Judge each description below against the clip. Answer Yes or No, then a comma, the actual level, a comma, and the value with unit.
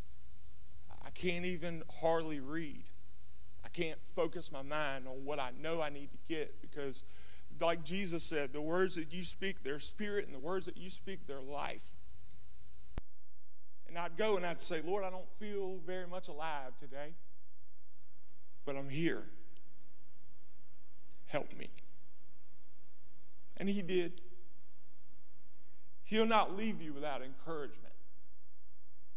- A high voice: No, low, 135 Hz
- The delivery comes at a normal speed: No, slow, 130 wpm